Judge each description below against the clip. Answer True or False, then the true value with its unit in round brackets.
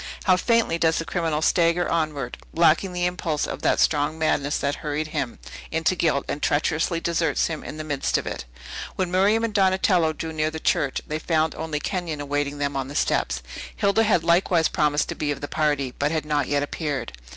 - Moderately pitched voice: True (155 Hz)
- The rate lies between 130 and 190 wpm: False (205 wpm)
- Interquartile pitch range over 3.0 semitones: False (2.7 semitones)